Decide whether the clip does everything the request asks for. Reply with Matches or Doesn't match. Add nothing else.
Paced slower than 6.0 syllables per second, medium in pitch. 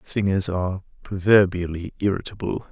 Doesn't match